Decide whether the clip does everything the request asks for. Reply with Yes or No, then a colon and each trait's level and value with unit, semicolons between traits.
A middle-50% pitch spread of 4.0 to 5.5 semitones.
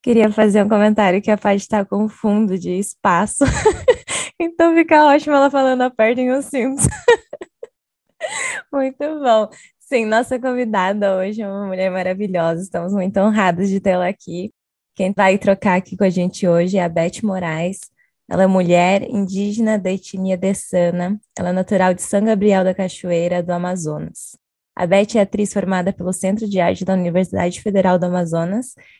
No: average, 3.0 semitones